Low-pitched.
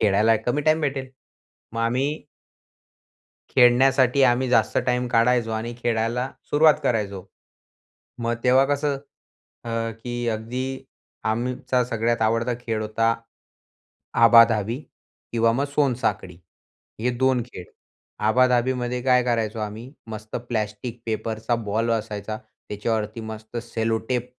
Yes: low, 115 Hz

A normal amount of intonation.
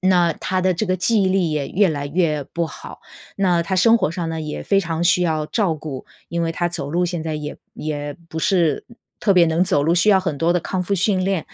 Yes: average, 3.0 semitones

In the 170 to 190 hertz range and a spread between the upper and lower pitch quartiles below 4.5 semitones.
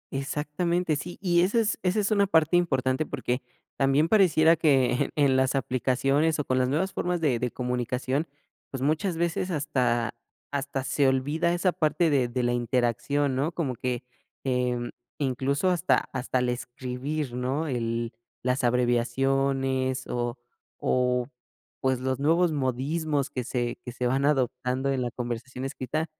No: low, 135 Hz; average, 3.7 semitones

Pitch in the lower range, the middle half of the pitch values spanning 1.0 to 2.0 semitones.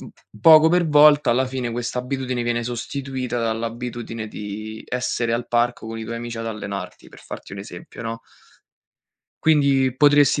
No: low, 120 Hz; average, 2.7 semitones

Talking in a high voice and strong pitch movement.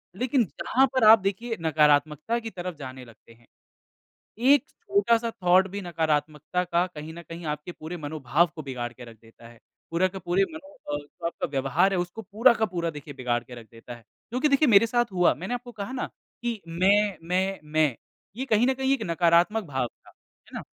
No: medium, 175 Hz; wide, 7.0 semitones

